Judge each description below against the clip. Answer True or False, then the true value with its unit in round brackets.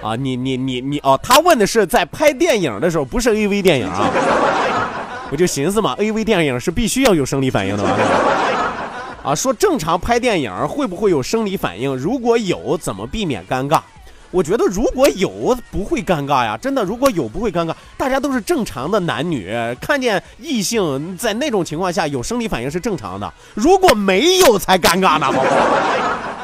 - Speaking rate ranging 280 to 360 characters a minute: True (285 characters per minute)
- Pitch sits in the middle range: False (200 Hz)